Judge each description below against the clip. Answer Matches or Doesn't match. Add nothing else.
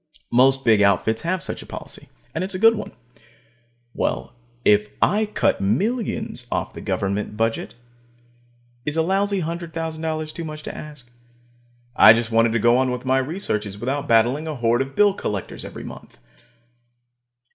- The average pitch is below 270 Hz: Matches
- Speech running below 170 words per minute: Matches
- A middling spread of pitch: Doesn't match